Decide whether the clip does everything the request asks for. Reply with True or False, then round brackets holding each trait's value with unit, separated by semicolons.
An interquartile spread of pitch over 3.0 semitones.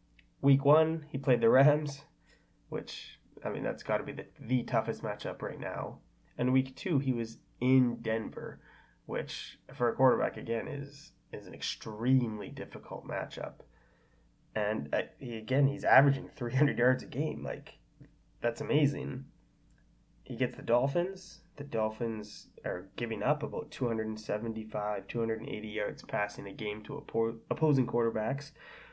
True (3.9 semitones)